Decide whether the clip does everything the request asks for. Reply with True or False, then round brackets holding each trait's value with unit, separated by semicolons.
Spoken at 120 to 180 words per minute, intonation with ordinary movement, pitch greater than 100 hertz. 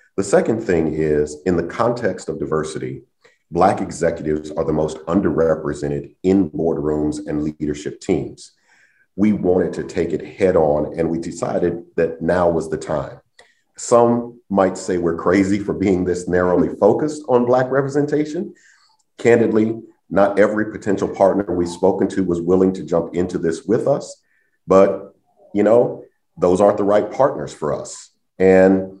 False (155 wpm; 3.8 semitones; 90 Hz)